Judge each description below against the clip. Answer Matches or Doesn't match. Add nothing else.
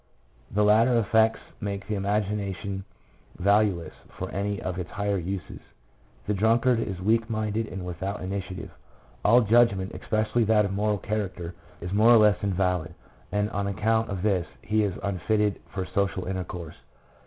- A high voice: Doesn't match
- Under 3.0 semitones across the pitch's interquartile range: Matches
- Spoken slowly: Doesn't match